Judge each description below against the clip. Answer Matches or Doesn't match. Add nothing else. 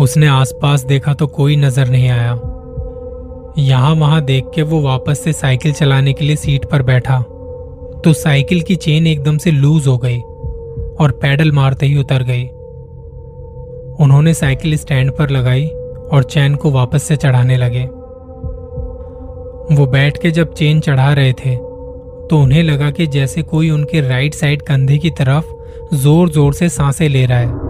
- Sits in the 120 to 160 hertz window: Matches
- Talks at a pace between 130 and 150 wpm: Doesn't match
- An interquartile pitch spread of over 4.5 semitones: Doesn't match